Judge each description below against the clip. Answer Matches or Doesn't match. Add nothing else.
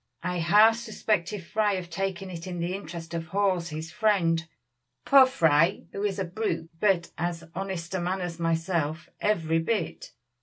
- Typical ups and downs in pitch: Matches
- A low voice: Doesn't match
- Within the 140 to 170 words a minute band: Matches